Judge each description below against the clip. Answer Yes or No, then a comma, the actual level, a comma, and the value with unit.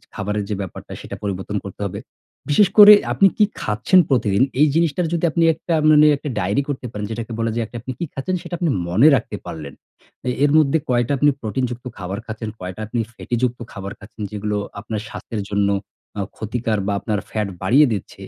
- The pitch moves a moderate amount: No, wide, 5.8 semitones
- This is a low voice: Yes, low, 115 Hz